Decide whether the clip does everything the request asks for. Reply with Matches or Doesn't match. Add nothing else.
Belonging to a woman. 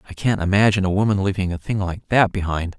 Doesn't match